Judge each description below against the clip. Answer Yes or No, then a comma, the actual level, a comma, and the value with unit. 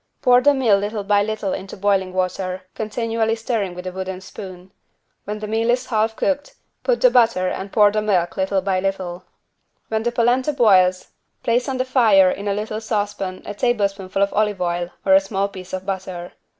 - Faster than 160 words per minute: Yes, average, 195 wpm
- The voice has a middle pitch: No, high, 205 Hz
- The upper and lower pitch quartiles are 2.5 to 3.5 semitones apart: Yes, average, 3.1 semitones